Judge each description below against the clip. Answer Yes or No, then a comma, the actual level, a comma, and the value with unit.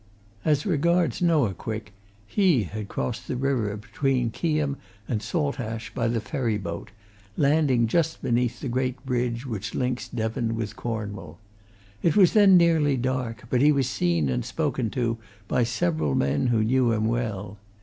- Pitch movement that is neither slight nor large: Yes, average, 4.2 semitones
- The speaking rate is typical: Yes, average, 160 wpm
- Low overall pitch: Yes, low, 120 Hz